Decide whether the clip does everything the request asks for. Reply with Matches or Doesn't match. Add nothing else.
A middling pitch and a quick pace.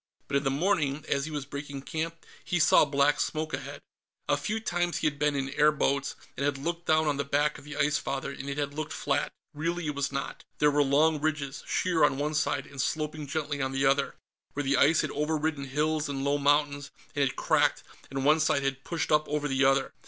Matches